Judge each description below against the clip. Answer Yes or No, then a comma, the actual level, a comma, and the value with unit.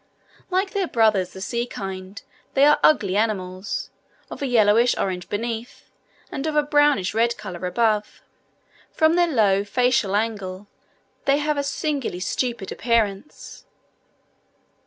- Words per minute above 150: No, slow, 135 wpm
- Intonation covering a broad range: Yes, wide, 6.1 semitones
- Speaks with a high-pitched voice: Yes, high, 225 Hz